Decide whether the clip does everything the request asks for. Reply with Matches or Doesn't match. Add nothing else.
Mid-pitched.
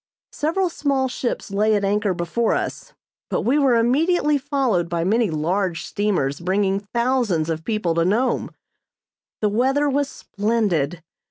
Doesn't match